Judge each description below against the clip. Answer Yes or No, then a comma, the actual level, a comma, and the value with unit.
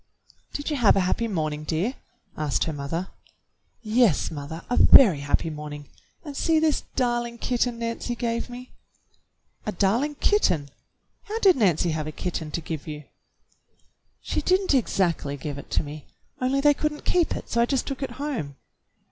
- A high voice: Yes, high, 220 Hz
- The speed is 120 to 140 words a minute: No, average, 175 wpm